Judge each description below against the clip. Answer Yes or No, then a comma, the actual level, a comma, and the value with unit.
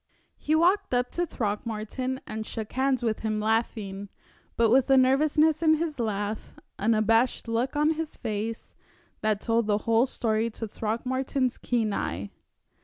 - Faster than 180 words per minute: No, average, 155 wpm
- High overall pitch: Yes, high, 230 Hz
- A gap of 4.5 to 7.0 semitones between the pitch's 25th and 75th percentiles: No, average, 3.5 semitones